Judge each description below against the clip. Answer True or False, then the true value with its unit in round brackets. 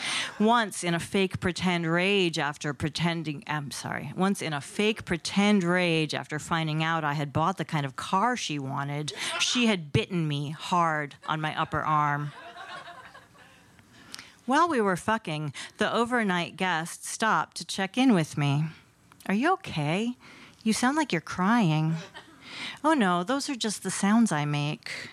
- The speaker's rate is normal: True (160 wpm)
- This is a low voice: False (175 Hz)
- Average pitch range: False (6.0 semitones)